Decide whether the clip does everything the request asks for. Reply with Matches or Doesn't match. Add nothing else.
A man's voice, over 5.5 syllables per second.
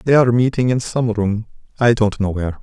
Matches